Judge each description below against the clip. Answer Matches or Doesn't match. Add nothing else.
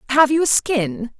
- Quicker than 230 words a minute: Doesn't match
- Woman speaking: Matches